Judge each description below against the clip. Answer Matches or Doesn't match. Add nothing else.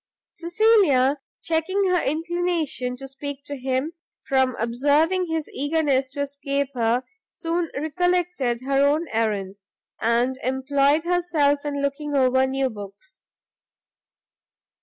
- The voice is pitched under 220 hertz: Doesn't match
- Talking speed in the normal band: Doesn't match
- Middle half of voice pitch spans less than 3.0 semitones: Doesn't match